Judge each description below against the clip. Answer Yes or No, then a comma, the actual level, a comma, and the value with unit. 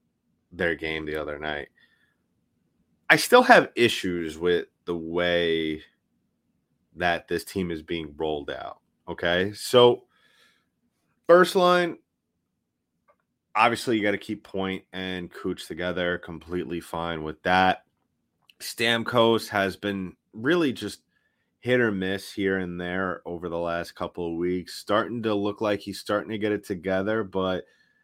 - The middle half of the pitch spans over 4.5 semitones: No, average, 3.3 semitones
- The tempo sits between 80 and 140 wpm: Yes, slow, 135 wpm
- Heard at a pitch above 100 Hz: No, very low, 95 Hz